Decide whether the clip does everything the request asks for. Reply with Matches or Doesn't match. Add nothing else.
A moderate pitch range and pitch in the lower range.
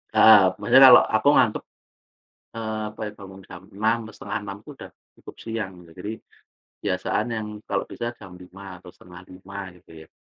Matches